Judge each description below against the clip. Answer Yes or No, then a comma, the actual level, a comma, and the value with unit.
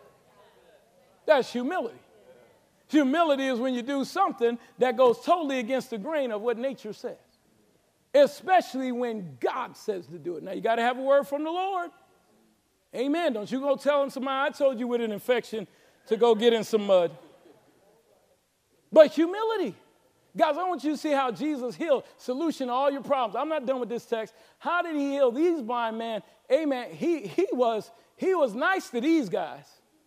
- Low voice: No, very high, 265 Hz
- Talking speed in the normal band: Yes, average, 185 wpm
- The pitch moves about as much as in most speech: Yes, average, 4.7 semitones